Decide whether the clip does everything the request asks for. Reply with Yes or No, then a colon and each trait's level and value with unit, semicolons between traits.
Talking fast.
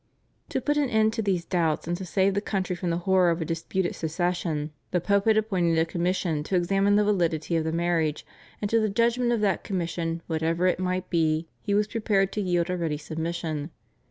Yes: fast, 215 wpm